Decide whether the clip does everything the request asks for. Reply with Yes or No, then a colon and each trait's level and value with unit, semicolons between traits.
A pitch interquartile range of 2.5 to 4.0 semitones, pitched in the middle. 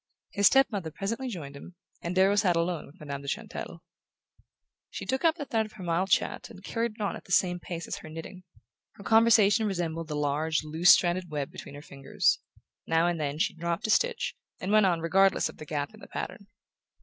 No: average, 4.7 semitones; medium, 175 Hz